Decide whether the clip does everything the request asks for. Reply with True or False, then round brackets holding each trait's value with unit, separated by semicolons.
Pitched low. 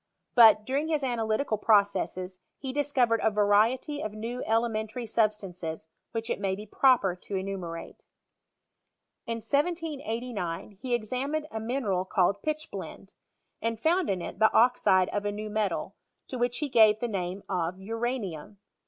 False (220 Hz)